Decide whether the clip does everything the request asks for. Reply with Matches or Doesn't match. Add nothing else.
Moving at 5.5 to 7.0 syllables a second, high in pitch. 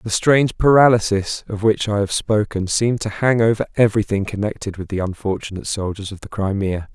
Doesn't match